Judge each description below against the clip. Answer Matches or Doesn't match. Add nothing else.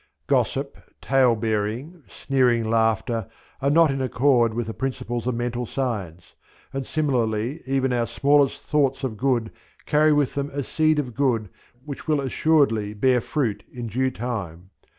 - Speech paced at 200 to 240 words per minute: Doesn't match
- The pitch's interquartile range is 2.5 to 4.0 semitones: Matches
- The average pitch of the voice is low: Matches